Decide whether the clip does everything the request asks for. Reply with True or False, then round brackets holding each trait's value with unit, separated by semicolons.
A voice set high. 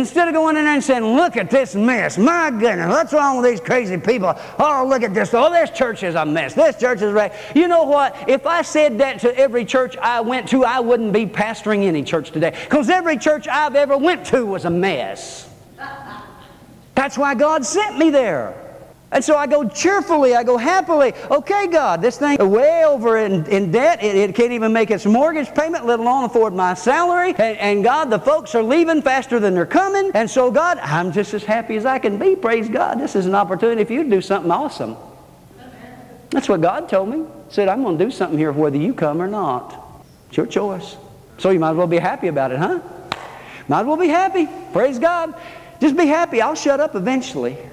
True (250 Hz)